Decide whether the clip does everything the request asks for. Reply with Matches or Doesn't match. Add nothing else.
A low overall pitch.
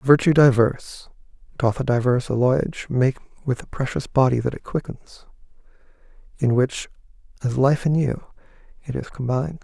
Matches